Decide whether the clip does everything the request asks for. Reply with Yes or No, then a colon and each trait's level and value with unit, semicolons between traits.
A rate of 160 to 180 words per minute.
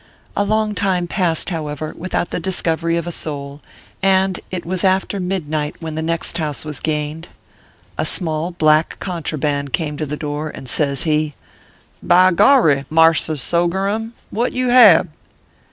Yes: average, 165 wpm